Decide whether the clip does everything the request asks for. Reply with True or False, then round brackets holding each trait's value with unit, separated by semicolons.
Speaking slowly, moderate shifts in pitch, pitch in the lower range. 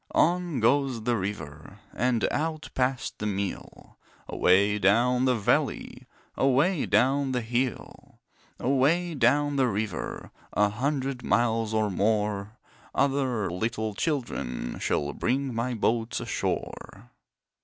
True (115 wpm; 4.3 semitones; 120 Hz)